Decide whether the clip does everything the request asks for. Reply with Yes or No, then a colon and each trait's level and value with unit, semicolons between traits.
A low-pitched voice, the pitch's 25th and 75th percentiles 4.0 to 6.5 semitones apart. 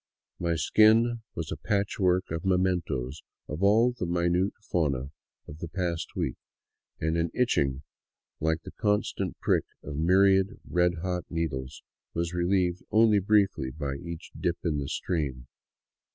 No: very low, 85 Hz; average, 3.5 semitones